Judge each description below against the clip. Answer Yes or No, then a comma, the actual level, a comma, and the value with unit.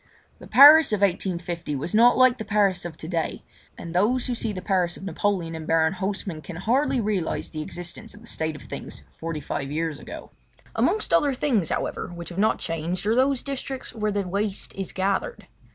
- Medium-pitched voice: No, high, 195 Hz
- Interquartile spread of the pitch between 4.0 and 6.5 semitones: Yes, average, 5.1 semitones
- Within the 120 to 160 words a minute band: No, average, 200 wpm